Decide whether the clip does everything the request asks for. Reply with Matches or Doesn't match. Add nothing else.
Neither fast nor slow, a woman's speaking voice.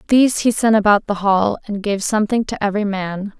Doesn't match